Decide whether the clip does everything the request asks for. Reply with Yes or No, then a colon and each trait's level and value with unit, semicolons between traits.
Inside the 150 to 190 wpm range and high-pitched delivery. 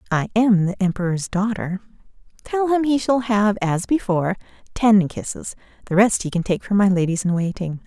Yes: average, 185 wpm; high, 200 Hz